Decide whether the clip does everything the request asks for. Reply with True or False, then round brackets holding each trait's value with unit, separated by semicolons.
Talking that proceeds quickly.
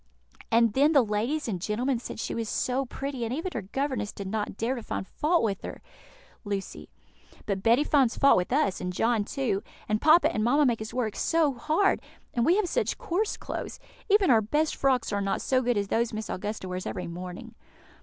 True (215 wpm)